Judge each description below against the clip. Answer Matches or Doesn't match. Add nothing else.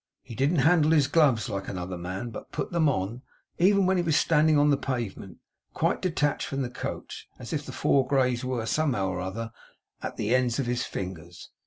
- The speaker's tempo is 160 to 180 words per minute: Doesn't match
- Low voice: Matches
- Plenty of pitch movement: Matches